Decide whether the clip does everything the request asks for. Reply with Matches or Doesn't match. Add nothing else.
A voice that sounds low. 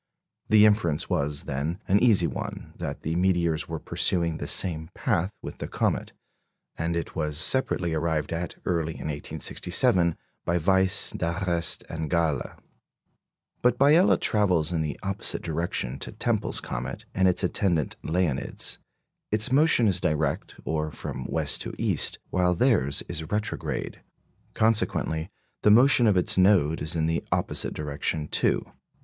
Matches